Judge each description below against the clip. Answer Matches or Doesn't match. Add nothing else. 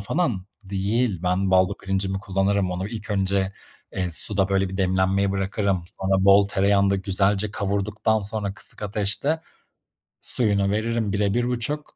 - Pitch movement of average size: Doesn't match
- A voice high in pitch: Doesn't match